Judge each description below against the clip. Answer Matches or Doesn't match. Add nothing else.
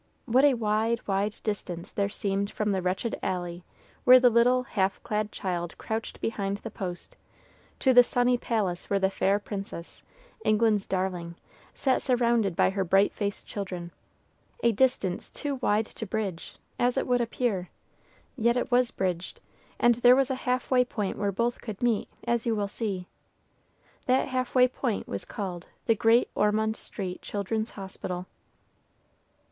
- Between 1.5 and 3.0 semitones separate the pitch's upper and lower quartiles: Doesn't match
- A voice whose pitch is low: Doesn't match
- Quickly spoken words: Doesn't match